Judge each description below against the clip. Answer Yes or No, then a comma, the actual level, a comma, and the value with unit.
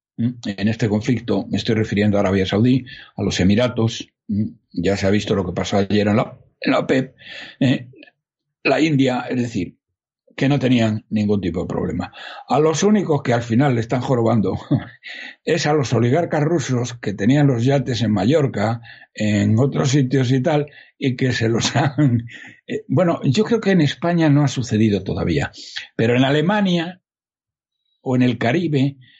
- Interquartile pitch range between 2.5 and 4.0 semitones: No, average, 4.8 semitones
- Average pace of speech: Yes, average, 175 wpm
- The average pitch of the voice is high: No, low, 125 Hz